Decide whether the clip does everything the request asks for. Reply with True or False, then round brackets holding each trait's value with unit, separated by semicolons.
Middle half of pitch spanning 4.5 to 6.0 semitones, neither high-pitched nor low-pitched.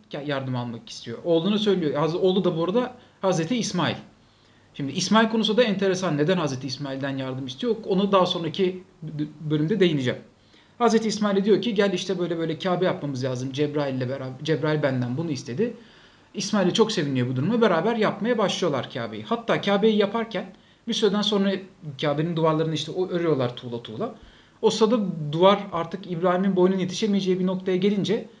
True (5.6 semitones; 180 Hz)